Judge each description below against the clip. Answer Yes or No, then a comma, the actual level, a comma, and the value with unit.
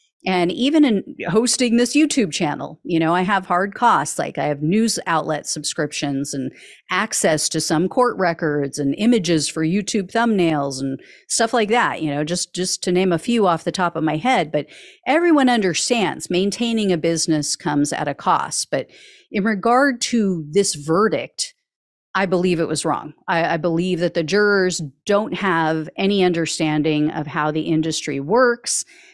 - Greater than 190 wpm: No, average, 175 wpm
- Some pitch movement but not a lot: No, wide, 6.2 semitones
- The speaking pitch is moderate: Yes, medium, 180 Hz